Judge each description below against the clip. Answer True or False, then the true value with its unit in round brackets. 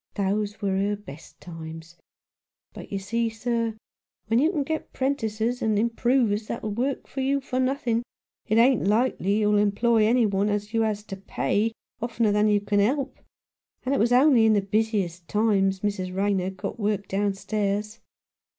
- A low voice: False (215 Hz)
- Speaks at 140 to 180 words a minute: True (170 wpm)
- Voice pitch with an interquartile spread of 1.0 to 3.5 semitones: True (2.7 semitones)